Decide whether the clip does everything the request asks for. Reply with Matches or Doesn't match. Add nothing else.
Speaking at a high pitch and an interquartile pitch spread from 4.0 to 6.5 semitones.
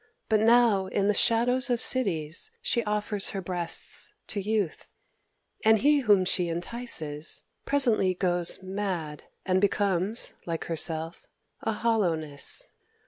Matches